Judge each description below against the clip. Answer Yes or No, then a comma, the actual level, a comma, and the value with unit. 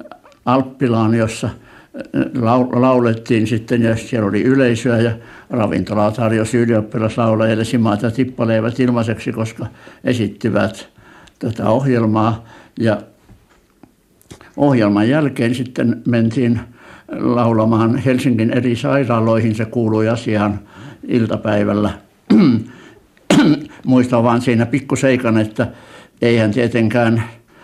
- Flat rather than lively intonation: Yes, narrow, 1.9 semitones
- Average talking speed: No, slow, 85 wpm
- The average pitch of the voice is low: Yes, low, 115 Hz